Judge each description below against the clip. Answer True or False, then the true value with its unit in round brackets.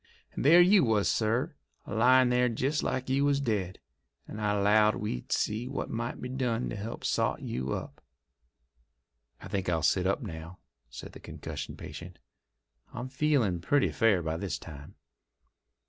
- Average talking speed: True (165 wpm)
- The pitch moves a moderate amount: False (5.8 semitones)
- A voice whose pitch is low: True (110 Hz)